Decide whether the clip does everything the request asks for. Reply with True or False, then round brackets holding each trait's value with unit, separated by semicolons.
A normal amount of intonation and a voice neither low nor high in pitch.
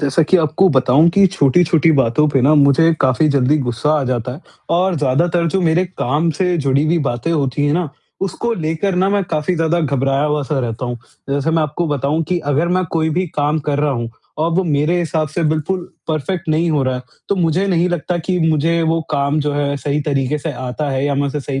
True (3.3 semitones; 150 Hz)